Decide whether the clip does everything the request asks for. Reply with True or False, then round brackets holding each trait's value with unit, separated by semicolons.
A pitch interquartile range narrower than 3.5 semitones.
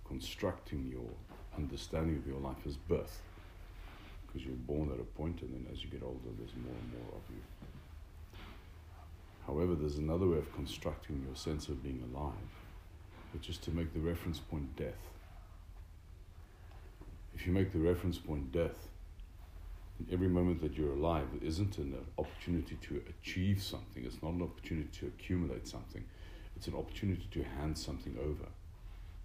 True (2.8 semitones)